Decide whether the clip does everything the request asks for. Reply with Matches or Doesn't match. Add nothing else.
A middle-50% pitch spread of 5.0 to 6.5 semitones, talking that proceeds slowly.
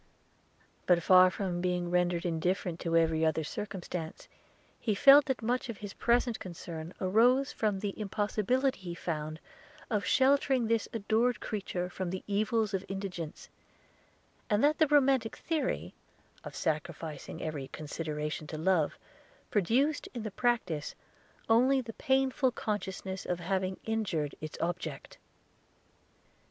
Matches